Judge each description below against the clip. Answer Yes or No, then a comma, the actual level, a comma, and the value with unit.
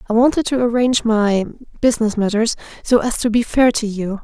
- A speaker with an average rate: Yes, average, 185 wpm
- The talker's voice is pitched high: Yes, high, 225 Hz